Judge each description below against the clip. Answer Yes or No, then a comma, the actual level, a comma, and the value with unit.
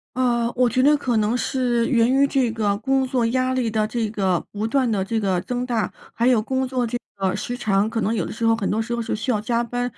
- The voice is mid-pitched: No, high, 235 Hz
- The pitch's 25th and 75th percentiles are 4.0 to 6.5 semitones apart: No, narrow, 2.6 semitones